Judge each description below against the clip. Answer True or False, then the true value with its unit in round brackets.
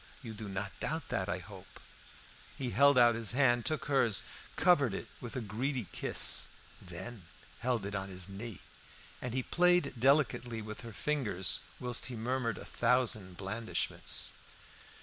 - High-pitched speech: False (115 Hz)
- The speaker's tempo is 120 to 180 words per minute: True (155 wpm)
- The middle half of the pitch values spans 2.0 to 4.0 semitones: False (4.4 semitones)